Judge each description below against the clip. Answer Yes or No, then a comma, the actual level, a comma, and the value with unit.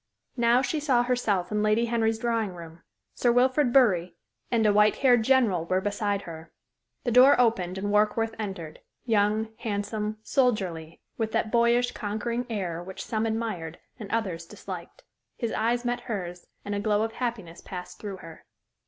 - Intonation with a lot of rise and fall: No, average, 3.8 semitones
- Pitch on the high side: Yes, high, 215 Hz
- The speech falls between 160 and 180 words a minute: Yes, average, 165 wpm